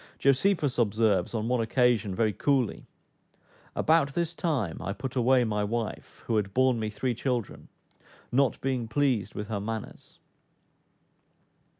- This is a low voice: Yes, low, 120 Hz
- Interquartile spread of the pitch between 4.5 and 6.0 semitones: No, average, 3.6 semitones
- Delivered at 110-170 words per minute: Yes, slow, 135 wpm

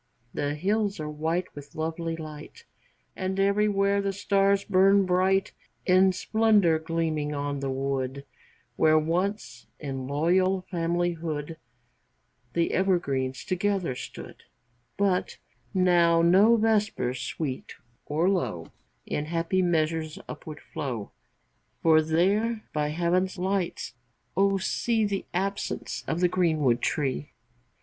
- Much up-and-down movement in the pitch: No, average, 4.2 semitones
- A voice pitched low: No, medium, 170 Hz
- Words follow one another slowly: Yes, slow, 115 wpm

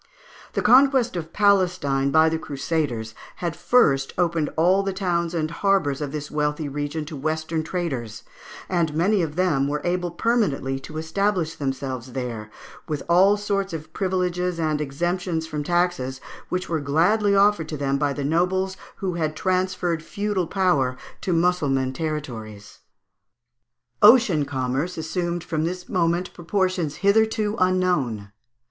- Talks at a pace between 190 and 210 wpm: No, average, 140 wpm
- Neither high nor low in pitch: Yes, medium, 165 Hz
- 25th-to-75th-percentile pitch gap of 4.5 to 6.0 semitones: No, average, 4.1 semitones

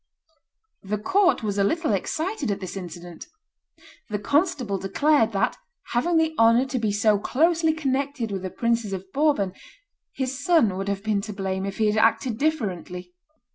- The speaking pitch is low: No, high, 220 Hz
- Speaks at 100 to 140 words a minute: No, average, 170 wpm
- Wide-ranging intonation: Yes, wide, 6.5 semitones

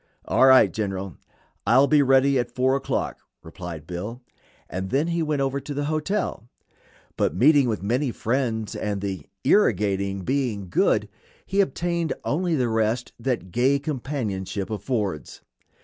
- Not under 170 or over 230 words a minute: No, average, 145 wpm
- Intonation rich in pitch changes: Yes, wide, 5.8 semitones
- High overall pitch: No, low, 125 Hz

